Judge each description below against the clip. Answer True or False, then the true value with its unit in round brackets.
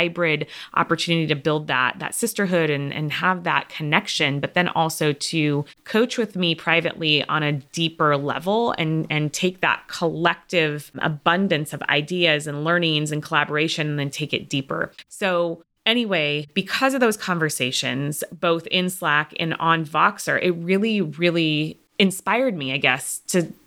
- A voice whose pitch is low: False (165 Hz)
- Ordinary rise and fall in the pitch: True (3.2 semitones)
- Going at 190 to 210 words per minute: False (155 wpm)